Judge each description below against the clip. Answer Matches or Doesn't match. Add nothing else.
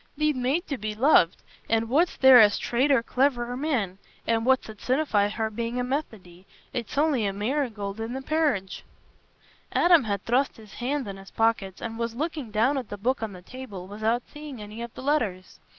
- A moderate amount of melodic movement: Matches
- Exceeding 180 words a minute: Matches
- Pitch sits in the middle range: Doesn't match